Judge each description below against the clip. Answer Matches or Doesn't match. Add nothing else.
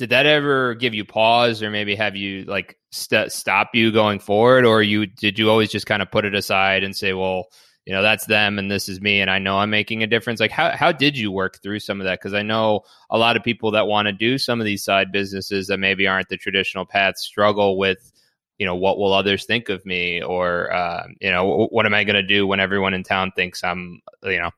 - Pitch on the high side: Doesn't match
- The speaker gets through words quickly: Matches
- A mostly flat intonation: Matches